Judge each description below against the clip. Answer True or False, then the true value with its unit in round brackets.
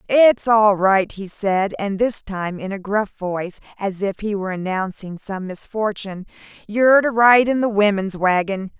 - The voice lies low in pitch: False (205 Hz)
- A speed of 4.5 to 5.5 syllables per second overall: True (4.6 syllables/s)